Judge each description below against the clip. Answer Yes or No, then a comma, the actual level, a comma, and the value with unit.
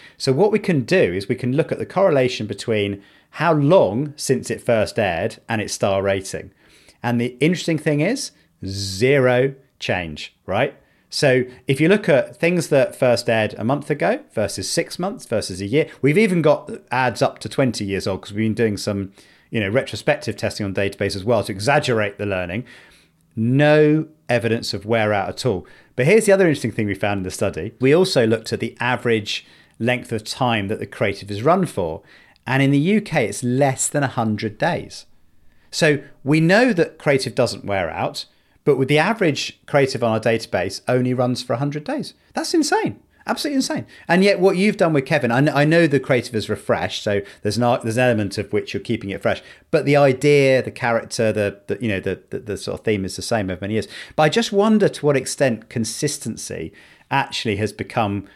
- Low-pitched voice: Yes, low, 120 Hz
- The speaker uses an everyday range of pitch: No, wide, 5.8 semitones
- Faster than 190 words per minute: Yes, fast, 205 wpm